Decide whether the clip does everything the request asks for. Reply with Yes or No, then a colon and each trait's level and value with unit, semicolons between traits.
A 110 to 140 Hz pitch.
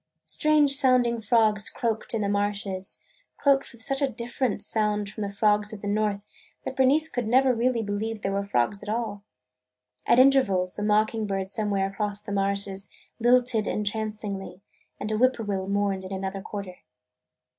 No: high, 210 Hz